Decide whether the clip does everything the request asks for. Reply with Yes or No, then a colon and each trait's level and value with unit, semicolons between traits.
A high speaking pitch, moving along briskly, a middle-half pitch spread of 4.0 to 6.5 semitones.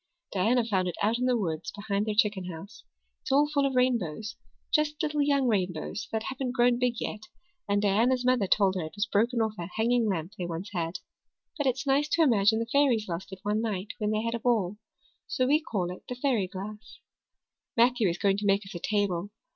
Yes: high, 215 Hz; fast, 220 wpm; average, 4.3 semitones